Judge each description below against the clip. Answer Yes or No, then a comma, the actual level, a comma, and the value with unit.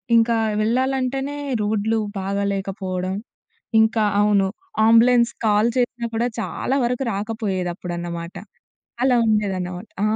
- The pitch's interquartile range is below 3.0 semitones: No, average, 3.6 semitones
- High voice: Yes, high, 215 Hz